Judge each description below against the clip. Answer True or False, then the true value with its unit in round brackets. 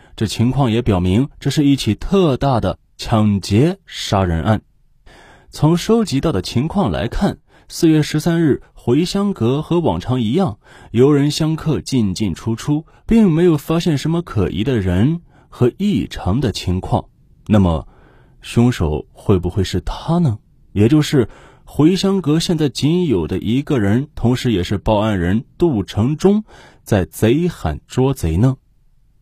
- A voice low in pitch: True (130 Hz)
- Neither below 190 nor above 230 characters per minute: True (215 characters per minute)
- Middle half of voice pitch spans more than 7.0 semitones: False (6.6 semitones)